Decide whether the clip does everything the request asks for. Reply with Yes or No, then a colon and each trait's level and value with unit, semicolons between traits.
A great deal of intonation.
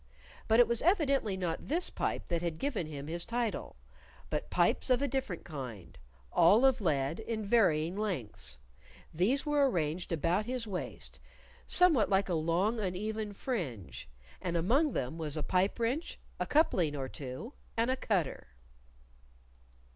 Yes: wide, 7.0 semitones